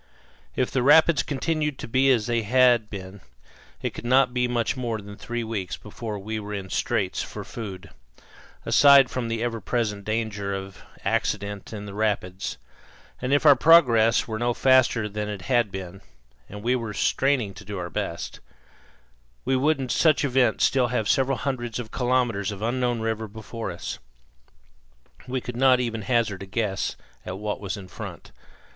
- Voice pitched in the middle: No, low, 115 Hz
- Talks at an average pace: Yes, average, 175 wpm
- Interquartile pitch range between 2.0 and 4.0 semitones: Yes, average, 3.7 semitones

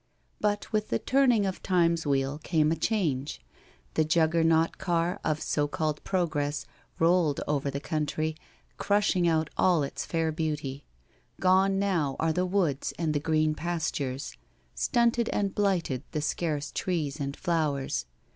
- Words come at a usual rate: Yes, average, 145 wpm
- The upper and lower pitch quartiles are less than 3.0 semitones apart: No, average, 3.7 semitones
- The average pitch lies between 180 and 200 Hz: No, medium, 160 Hz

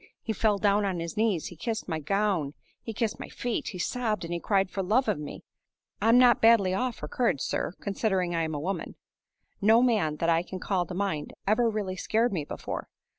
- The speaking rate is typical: No, fast, 210 wpm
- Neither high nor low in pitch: No, high, 200 Hz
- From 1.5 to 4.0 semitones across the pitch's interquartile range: No, average, 4.4 semitones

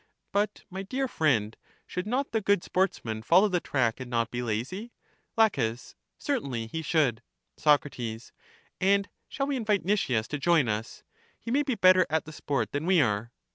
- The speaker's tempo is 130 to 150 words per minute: No, average, 175 wpm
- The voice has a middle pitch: Yes, medium, 170 Hz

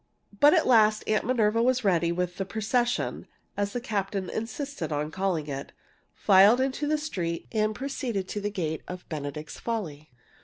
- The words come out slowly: No, average, 165 wpm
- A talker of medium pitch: No, high, 205 Hz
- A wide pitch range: Yes, wide, 5.7 semitones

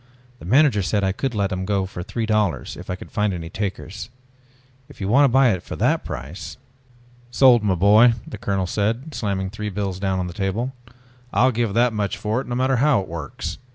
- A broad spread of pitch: No, average, 4.0 semitones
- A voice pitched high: No, low, 105 Hz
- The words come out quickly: Yes, fast, 220 wpm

